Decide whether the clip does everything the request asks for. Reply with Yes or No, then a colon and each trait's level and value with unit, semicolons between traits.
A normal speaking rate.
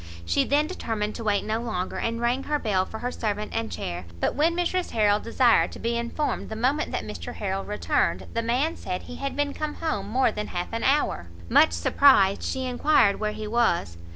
No: fast, 210 wpm